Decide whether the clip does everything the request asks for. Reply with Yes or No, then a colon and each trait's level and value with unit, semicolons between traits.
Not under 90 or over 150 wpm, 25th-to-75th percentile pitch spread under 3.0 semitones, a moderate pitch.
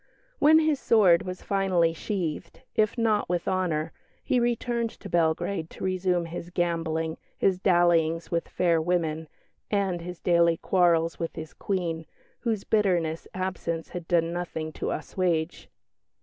Yes: average, 140 wpm; narrow, 2.6 semitones; medium, 175 Hz